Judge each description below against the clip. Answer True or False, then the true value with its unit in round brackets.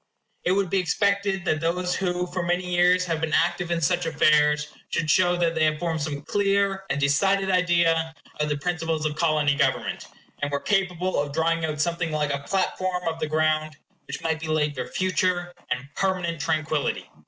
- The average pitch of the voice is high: False (165 Hz)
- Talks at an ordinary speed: True (190 wpm)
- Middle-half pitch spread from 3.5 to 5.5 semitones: False (2.9 semitones)